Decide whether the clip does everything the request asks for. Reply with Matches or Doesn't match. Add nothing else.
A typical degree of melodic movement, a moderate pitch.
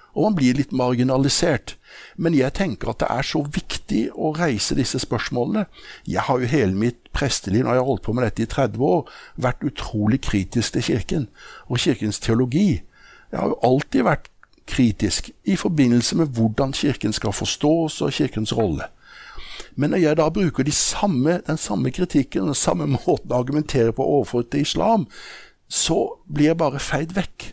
Doesn't match